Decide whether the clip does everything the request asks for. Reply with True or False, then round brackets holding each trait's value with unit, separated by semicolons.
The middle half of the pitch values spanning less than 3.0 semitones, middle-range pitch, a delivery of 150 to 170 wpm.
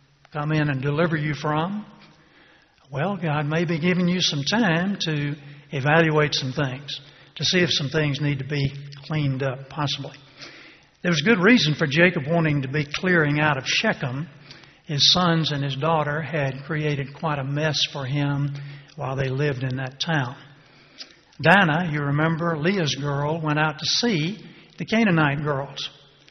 True (2.6 semitones; 150 Hz; 165 wpm)